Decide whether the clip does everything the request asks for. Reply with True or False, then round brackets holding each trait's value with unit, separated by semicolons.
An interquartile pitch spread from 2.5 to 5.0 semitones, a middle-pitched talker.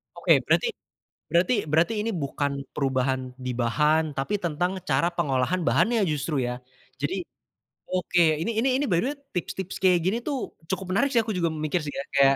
False (5.4 semitones; 170 Hz)